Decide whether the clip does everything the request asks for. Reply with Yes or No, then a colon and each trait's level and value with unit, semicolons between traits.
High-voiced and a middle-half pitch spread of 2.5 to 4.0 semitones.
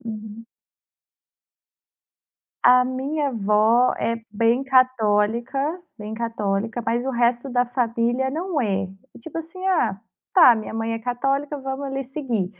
Yes: high, 245 Hz; average, 3.2 semitones